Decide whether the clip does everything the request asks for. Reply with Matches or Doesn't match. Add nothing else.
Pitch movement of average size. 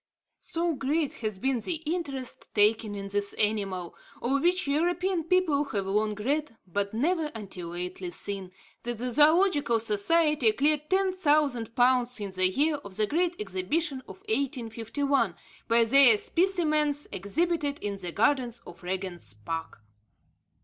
Doesn't match